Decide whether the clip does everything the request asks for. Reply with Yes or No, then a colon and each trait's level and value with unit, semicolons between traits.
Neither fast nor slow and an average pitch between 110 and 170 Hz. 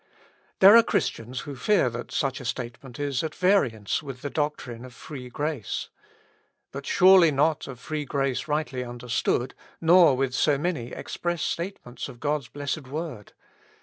Yes: average, 155 wpm; medium, 140 Hz